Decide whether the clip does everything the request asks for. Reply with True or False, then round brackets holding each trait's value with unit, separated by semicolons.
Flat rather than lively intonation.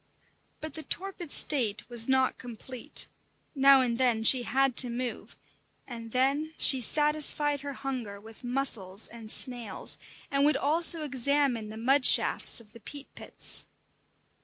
False (3.5 semitones)